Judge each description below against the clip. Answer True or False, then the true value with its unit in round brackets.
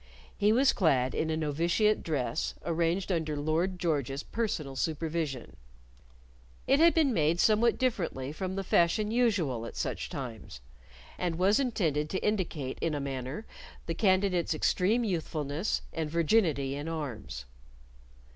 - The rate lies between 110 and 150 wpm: True (135 wpm)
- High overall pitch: False (165 Hz)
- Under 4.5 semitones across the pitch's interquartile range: False (5.3 semitones)